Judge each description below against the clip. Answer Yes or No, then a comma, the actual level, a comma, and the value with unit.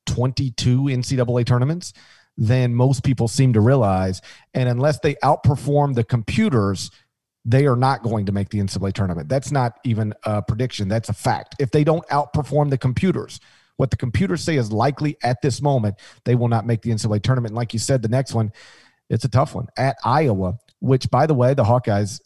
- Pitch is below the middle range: Yes, low, 125 Hz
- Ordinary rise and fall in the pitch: Yes, average, 3.3 semitones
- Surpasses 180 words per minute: Yes, average, 195 wpm